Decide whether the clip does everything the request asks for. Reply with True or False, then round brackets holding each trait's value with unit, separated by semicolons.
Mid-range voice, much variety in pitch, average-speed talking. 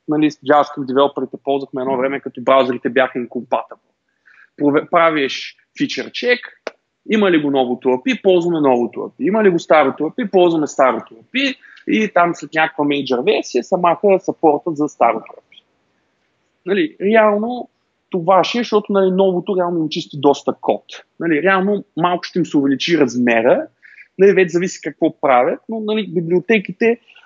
True (170 Hz; 5.8 semitones; 150 wpm)